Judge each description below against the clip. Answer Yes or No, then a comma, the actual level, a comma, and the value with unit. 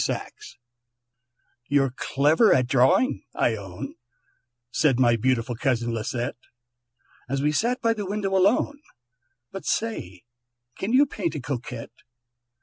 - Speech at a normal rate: No, slow, 125 wpm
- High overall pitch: No, medium, 140 Hz